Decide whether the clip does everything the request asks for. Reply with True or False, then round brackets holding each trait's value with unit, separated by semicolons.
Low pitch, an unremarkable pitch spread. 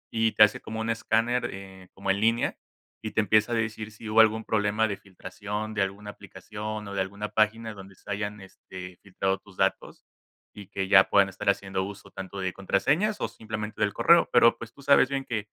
False (105 Hz; 2.3 semitones)